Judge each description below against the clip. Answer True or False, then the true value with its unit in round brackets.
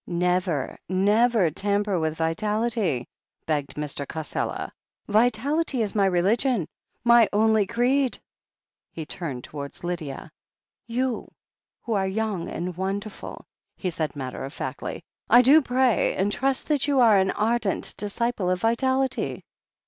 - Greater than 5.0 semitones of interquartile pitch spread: True (5.5 semitones)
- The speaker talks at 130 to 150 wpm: True (135 wpm)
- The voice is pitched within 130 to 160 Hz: False (205 Hz)